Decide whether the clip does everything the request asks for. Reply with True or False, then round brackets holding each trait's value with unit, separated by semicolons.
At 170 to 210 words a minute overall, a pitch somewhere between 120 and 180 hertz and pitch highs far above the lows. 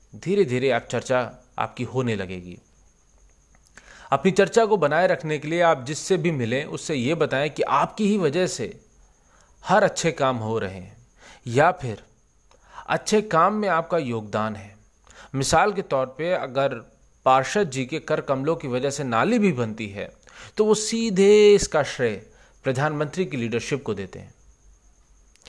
False (160 wpm; 135 Hz; 7.6 semitones)